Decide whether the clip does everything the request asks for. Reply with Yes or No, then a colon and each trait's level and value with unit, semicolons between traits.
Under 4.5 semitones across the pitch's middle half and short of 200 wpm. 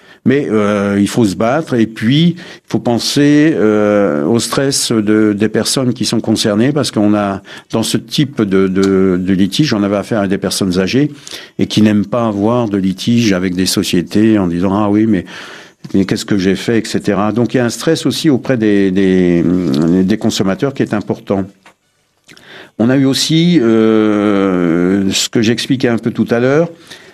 Yes: average, 3.4 semitones; average, 190 wpm